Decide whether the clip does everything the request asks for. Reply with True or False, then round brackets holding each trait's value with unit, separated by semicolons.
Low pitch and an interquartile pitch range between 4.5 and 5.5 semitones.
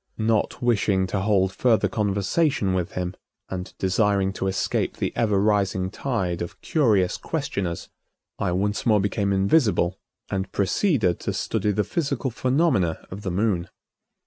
False (100 Hz; 3.3 semitones)